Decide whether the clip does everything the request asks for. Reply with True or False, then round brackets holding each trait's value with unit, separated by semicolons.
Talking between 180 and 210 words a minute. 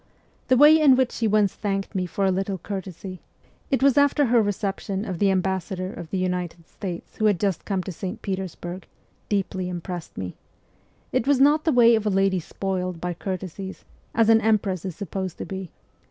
True (195 wpm)